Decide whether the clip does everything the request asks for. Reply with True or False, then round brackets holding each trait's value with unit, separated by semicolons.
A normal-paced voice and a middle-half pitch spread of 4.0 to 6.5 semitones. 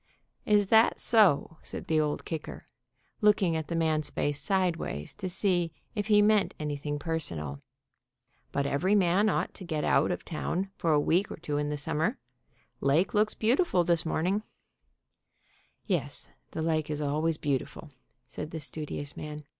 True (170 wpm; 4.5 semitones)